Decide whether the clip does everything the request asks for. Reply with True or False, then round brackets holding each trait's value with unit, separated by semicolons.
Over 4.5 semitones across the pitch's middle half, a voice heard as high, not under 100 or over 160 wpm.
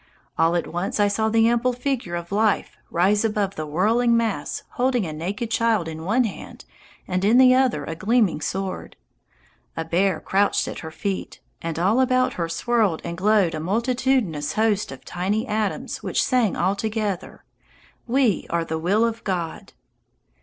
False (5.1 semitones; 205 Hz; 170 wpm)